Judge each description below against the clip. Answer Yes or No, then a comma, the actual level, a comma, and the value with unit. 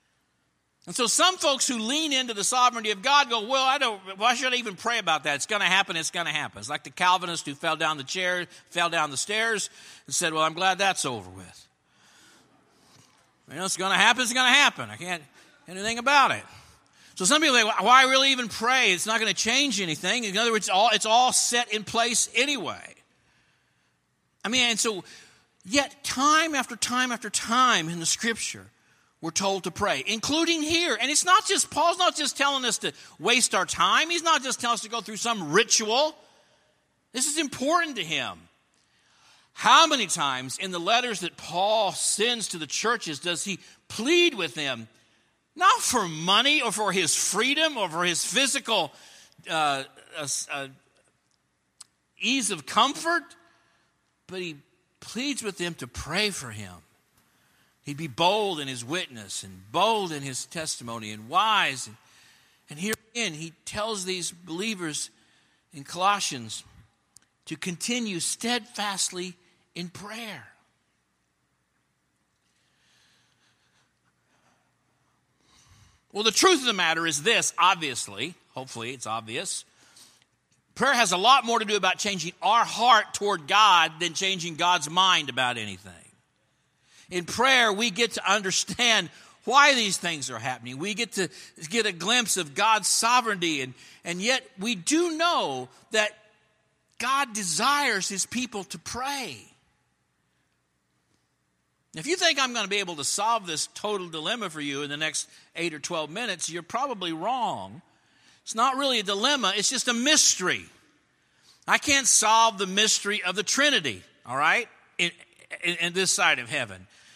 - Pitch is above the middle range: Yes, high, 200 Hz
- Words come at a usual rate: Yes, average, 165 wpm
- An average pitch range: No, wide, 6.7 semitones